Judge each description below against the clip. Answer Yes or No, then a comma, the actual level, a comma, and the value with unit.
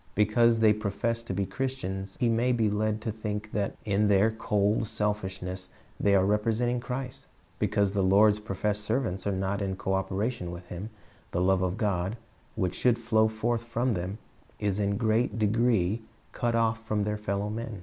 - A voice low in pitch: Yes, low, 105 Hz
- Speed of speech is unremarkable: Yes, average, 180 wpm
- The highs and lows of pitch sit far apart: No, average, 2.7 semitones